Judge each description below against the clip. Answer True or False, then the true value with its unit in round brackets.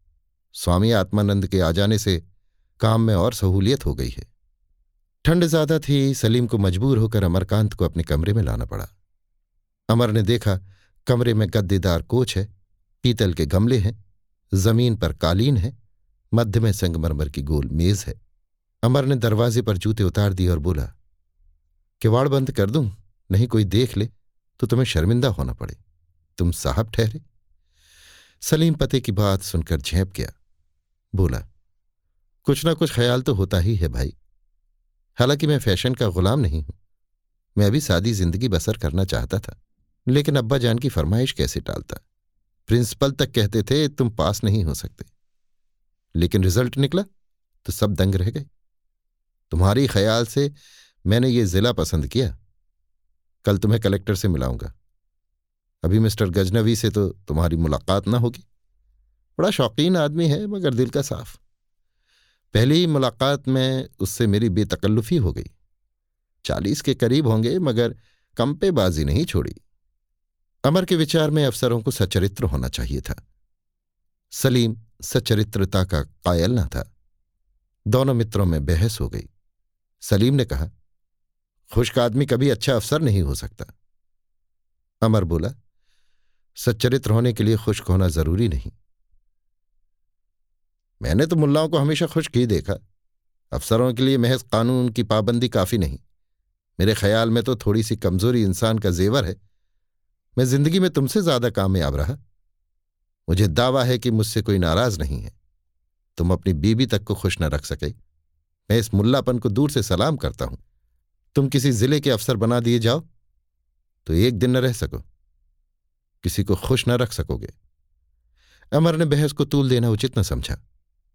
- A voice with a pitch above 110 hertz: False (105 Hz)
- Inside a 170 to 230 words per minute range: False (155 wpm)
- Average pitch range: False (6.0 semitones)